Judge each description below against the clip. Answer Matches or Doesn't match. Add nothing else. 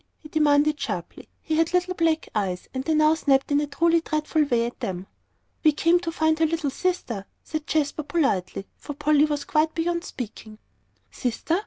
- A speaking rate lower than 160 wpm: Doesn't match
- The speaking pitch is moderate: Doesn't match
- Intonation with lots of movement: Doesn't match